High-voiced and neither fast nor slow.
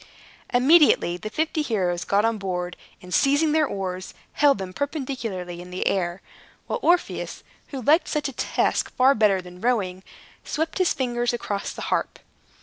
Yes: high, 225 Hz; average, 160 wpm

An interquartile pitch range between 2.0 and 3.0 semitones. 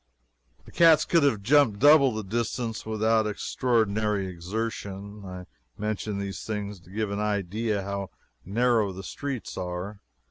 Yes: narrow, 2.5 semitones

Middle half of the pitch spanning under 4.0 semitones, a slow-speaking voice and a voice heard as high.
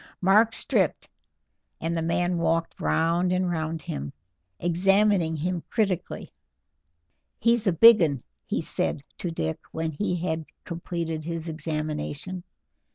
No: narrow, 2.4 semitones; slow, 125 wpm; medium, 170 Hz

